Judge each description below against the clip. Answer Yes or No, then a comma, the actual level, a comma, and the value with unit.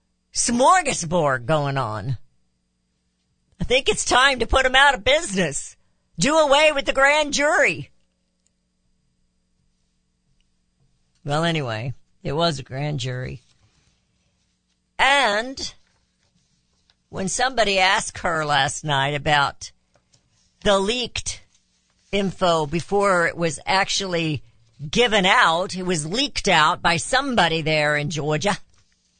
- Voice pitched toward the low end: No, medium, 155 Hz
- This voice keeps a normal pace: No, slow, 105 wpm